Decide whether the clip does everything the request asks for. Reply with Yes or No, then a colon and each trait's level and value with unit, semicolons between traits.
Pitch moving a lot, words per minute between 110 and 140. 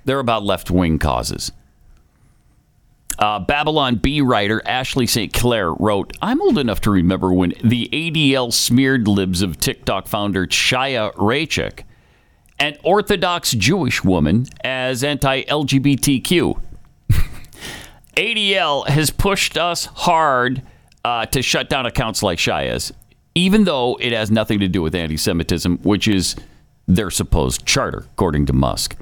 Yes: wide, 6.6 semitones; slow, 135 wpm